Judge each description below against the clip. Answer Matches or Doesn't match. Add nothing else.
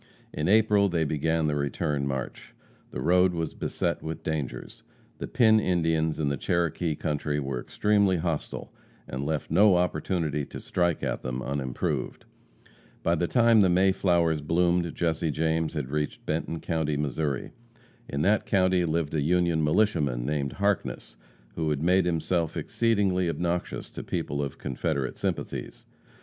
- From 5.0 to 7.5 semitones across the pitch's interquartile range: Doesn't match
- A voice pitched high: Doesn't match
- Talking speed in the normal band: Matches